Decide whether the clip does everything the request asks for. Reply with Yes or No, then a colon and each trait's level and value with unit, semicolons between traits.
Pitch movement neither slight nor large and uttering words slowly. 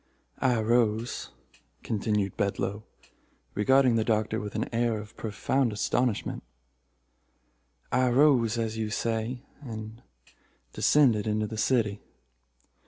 No: narrow, 2.3 semitones; slow, 105 wpm